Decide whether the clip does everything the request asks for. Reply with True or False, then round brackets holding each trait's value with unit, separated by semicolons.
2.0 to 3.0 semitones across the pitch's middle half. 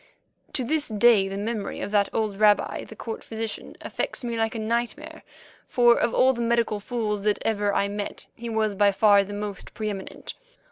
True (2.4 semitones)